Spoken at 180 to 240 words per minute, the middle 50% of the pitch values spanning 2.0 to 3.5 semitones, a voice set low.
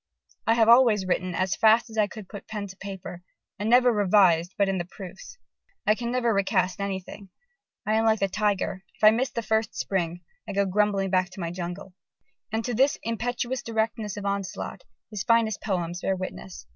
No: average, 195 wpm; average, 2.9 semitones; high, 205 Hz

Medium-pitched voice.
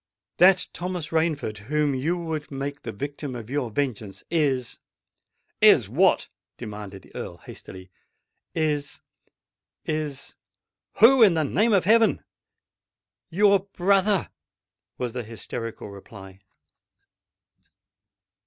Yes: medium, 145 Hz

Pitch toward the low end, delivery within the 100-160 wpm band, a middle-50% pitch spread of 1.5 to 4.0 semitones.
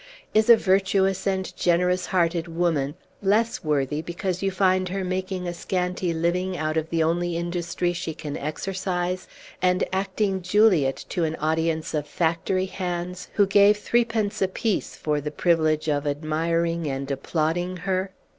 No: medium, 175 Hz; average, 150 wpm; average, 2.8 semitones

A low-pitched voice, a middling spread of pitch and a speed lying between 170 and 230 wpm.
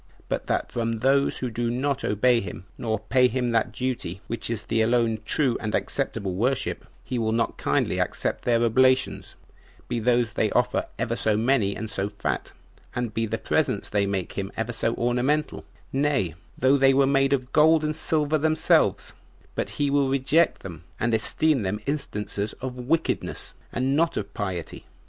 Yes: low, 120 Hz; average, 3.7 semitones; average, 175 wpm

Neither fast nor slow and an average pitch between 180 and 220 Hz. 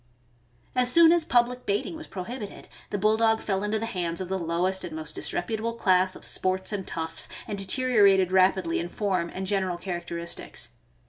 Yes: average, 175 wpm; high, 190 Hz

